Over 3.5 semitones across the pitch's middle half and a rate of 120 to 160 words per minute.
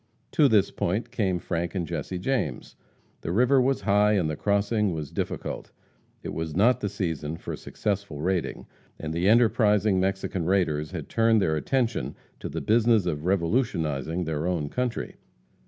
Yes: average, 4.9 semitones; average, 155 wpm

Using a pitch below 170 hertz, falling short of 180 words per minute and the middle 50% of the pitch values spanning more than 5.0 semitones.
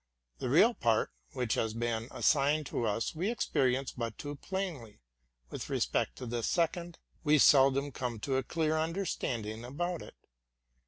Yes: low, 135 Hz; average, 160 wpm; wide, 5.6 semitones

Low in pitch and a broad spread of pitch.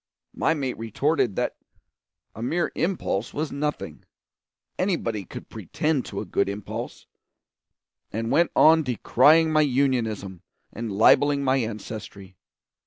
Yes: low, 130 Hz; wide, 5.9 semitones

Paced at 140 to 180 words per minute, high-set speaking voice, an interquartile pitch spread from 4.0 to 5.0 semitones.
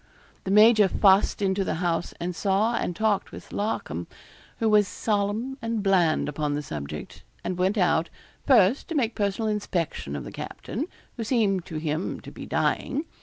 Yes: average, 170 wpm; high, 195 Hz; average, 4.3 semitones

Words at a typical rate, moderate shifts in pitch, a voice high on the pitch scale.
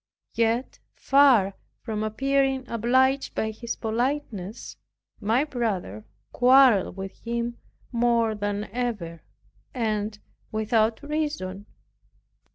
No: slow, 90 wpm; average, 3.6 semitones; high, 230 Hz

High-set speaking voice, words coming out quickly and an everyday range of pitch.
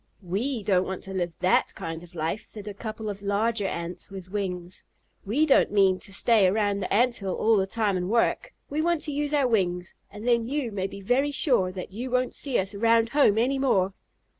Yes: high, 205 Hz; fast, 220 wpm; average, 4.3 semitones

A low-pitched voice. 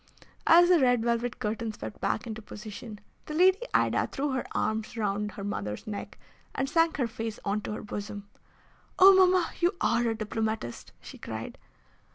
No: high, 225 Hz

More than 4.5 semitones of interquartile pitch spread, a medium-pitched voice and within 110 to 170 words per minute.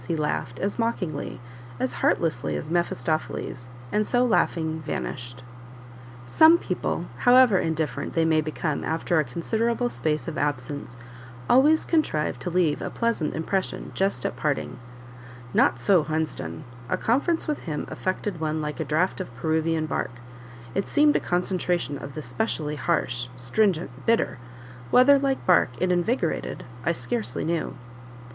Yes: wide, 5.6 semitones; medium, 160 Hz; average, 145 wpm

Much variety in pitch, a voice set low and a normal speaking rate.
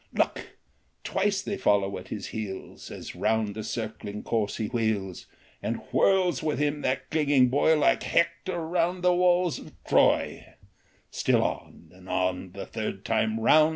Yes: wide, 8.0 semitones; low, 130 Hz; average, 155 wpm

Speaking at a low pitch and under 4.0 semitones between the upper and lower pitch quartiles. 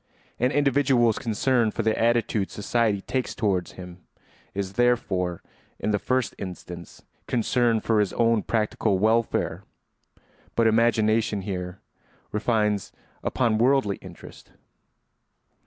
Yes: low, 110 Hz; average, 3.0 semitones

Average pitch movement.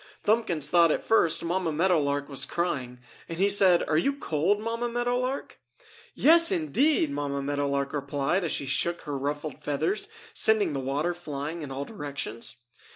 No: wide, 6.2 semitones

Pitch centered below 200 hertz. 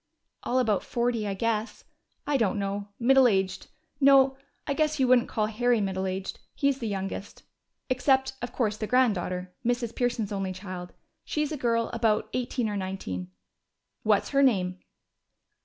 No: high, 225 Hz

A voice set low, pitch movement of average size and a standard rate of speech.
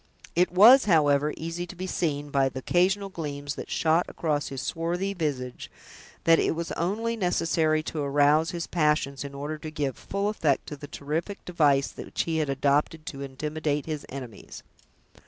No: medium, 155 Hz; average, 3.3 semitones; average, 175 wpm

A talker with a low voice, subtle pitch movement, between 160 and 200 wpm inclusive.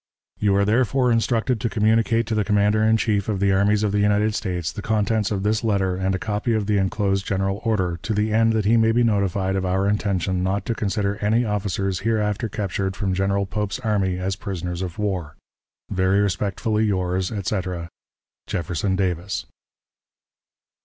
Yes: low, 100 Hz; narrow, 2.2 semitones; average, 180 wpm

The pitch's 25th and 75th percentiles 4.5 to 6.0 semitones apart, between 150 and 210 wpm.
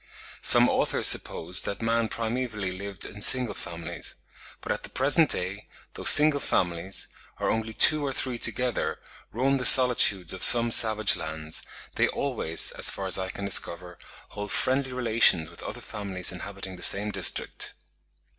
Yes: average, 5.0 semitones; average, 160 wpm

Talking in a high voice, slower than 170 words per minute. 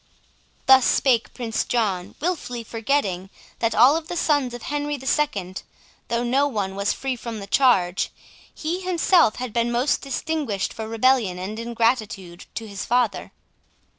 Yes: high, 235 Hz; average, 155 wpm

